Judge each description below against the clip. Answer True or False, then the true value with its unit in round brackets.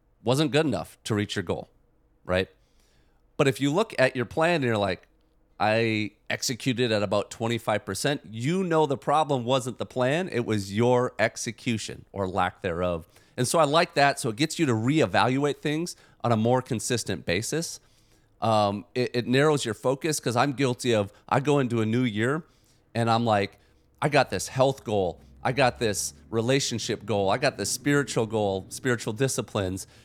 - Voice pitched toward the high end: False (120 Hz)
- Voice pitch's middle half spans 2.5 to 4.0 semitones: False (4.4 semitones)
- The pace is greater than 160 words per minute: True (180 wpm)